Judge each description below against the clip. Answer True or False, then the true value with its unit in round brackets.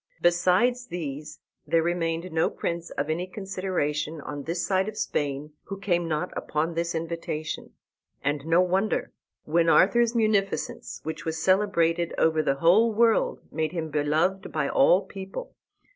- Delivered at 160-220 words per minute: False (145 wpm)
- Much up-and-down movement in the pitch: False (3.3 semitones)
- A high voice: False (170 Hz)